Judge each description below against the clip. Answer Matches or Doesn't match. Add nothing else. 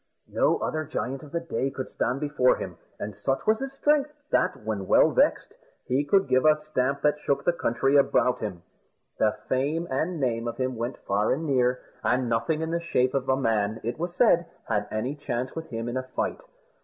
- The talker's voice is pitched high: Doesn't match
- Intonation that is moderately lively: Matches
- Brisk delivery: Matches